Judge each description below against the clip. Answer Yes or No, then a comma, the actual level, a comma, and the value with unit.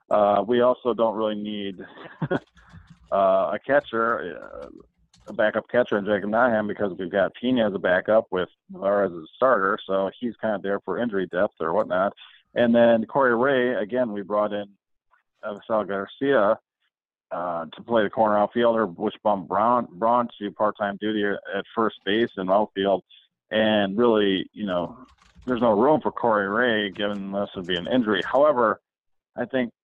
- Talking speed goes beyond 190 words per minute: No, average, 170 wpm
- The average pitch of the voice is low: Yes, low, 105 Hz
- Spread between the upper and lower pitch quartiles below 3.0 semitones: Yes, narrow, 2.6 semitones